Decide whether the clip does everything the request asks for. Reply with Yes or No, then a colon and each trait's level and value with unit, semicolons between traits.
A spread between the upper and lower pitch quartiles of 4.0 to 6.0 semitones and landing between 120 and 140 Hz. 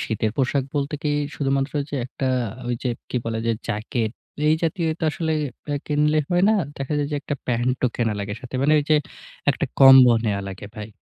Yes: average, 4.3 semitones; low, 135 Hz